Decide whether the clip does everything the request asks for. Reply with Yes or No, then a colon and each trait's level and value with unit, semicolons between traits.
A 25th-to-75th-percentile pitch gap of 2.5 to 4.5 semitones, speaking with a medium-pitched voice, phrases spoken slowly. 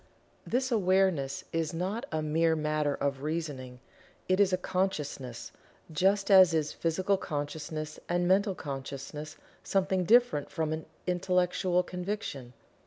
Yes: average, 4.0 semitones; medium, 165 Hz; slow, 125 wpm